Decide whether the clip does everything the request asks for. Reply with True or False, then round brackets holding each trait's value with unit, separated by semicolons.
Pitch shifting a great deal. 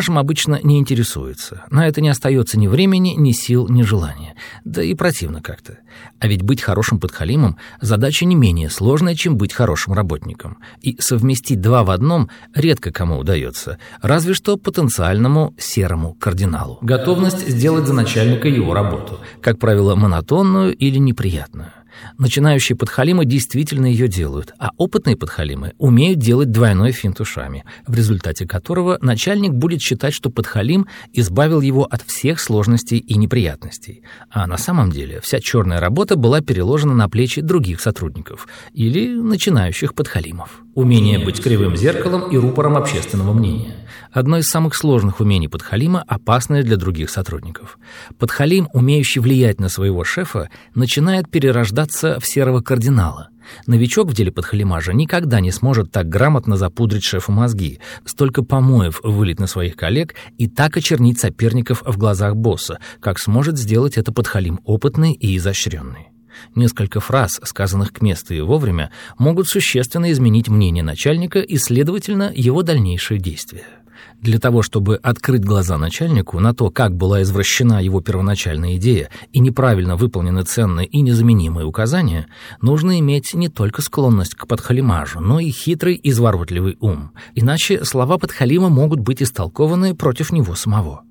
True (6.0 semitones)